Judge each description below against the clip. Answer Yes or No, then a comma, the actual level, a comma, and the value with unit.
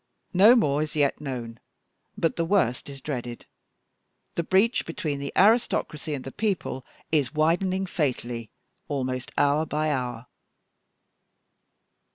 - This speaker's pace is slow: Yes, slow, 125 wpm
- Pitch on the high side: No, medium, 150 Hz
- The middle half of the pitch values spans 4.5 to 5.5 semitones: Yes, average, 4.8 semitones